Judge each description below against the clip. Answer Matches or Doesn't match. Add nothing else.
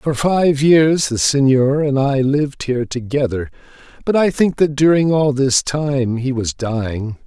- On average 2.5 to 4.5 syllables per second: Matches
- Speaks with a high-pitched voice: Doesn't match